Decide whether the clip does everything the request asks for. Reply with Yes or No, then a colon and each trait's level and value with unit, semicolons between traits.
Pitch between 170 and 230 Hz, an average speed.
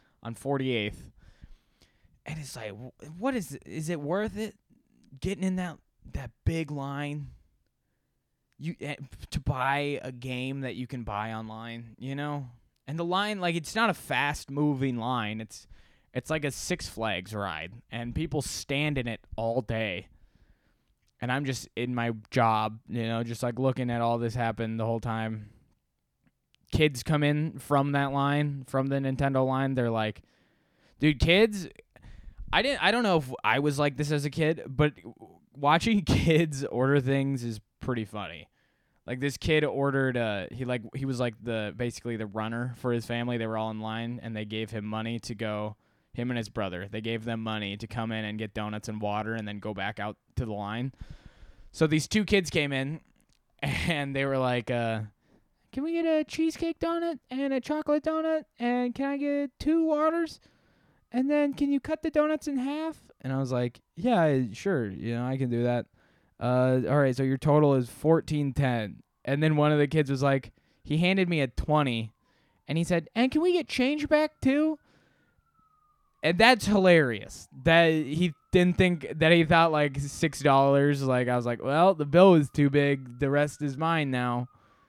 No: low, 135 Hz; average, 190 wpm